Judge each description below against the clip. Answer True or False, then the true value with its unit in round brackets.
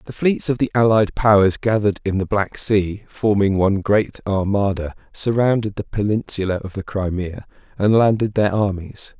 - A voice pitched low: True (100 Hz)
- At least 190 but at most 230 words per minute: False (165 wpm)